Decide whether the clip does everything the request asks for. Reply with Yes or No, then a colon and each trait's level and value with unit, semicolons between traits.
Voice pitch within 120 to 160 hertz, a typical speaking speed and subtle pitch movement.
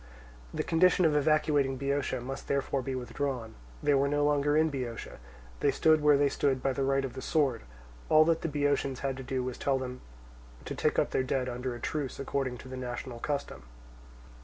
No: low, 135 Hz; fast, 210 wpm; narrow, 2.2 semitones